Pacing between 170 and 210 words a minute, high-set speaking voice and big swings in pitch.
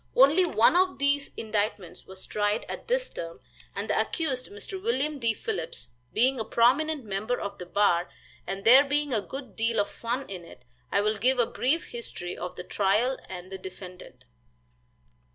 Yes: average, 180 wpm; high, 235 Hz; wide, 6.1 semitones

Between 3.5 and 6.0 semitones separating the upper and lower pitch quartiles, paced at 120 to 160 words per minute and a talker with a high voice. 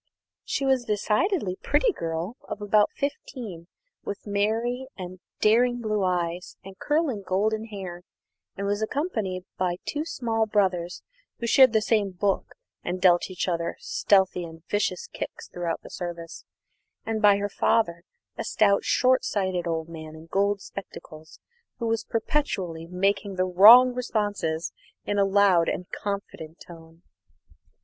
Yes: average, 3.9 semitones; average, 145 wpm; high, 200 Hz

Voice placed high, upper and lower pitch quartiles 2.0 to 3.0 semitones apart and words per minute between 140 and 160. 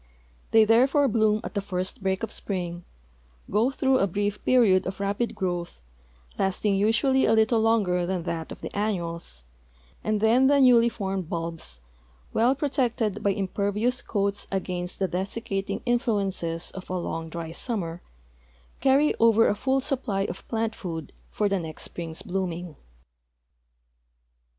No: high, 200 Hz; average, 4.2 semitones; average, 150 wpm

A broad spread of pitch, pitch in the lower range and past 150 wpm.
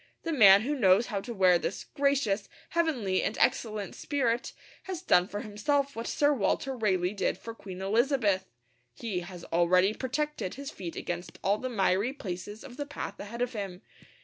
No: wide, 5.8 semitones; high, 215 Hz; average, 175 wpm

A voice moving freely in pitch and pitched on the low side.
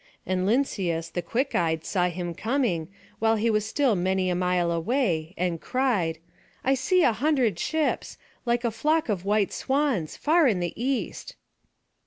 No: wide, 6.8 semitones; high, 210 Hz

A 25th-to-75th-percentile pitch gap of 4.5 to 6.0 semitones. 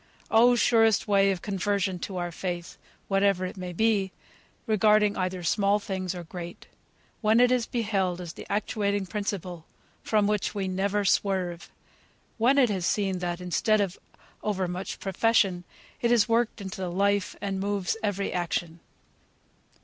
No: narrow, 2.5 semitones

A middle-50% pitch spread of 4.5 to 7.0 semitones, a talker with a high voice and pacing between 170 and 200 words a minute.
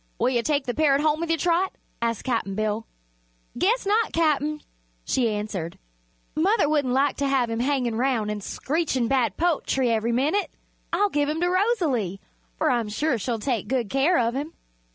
Yes: average, 5.2 semitones; very high, 270 Hz; average, 180 wpm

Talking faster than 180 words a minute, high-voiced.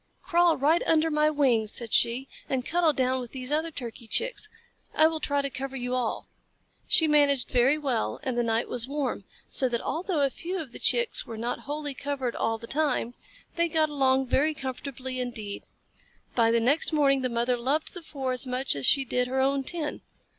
Yes: fast, 205 wpm; very high, 270 Hz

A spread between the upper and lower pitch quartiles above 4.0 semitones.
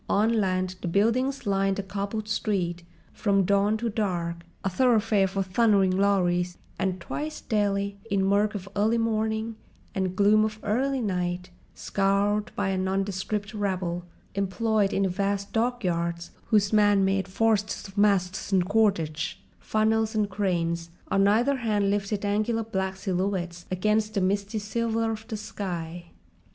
No: narrow, 2.4 semitones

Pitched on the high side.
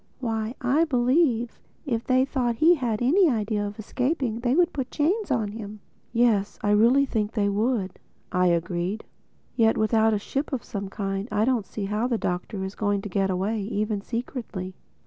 Yes: high, 225 Hz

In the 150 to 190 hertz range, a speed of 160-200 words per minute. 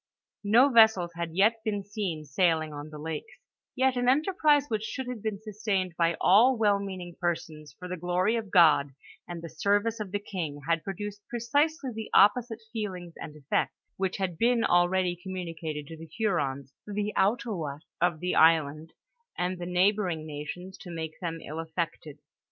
Yes: medium, 185 Hz; average, 170 wpm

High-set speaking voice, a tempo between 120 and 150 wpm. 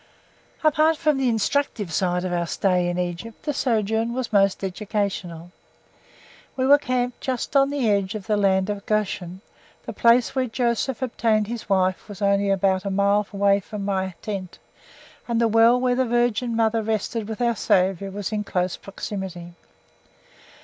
No: high, 210 Hz; average, 170 wpm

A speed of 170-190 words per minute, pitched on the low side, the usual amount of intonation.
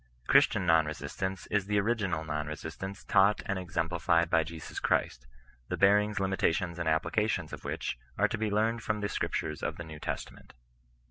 Yes: average, 175 wpm; very low, 90 Hz; average, 4.3 semitones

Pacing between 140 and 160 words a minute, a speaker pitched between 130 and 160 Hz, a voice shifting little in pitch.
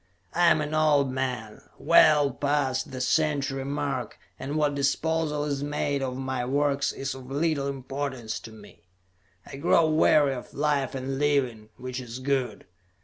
Yes: average, 155 wpm; medium, 140 Hz; narrow, 2.1 semitones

